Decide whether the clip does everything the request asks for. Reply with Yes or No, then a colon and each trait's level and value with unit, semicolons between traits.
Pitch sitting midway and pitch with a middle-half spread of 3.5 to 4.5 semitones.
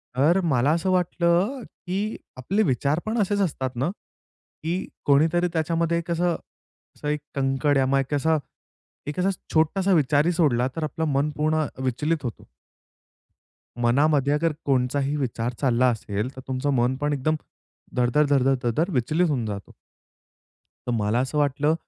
Yes: medium, 145 Hz; average, 4.1 semitones